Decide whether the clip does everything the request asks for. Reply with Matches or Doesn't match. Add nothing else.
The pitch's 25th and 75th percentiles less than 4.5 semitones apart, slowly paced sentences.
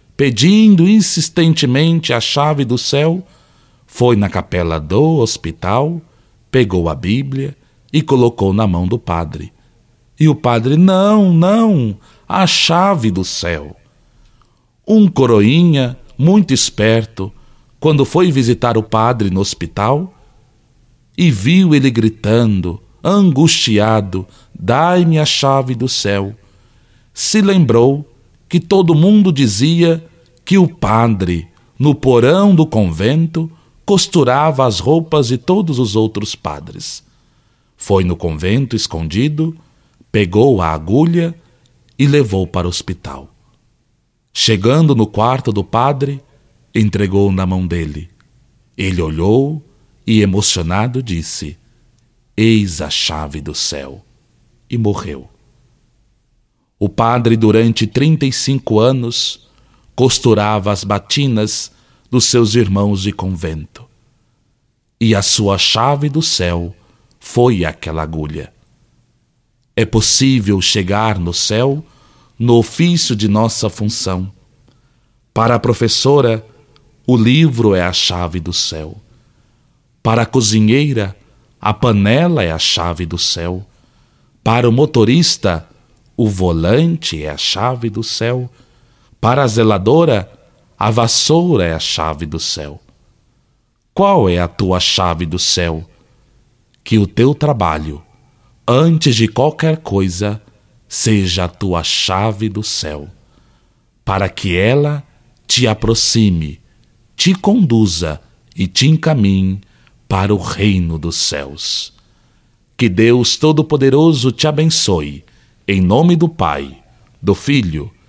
Doesn't match